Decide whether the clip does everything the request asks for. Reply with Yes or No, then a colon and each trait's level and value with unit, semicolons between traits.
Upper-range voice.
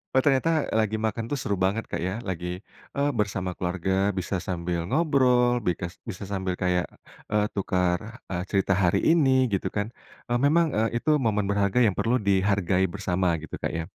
No: low, 100 Hz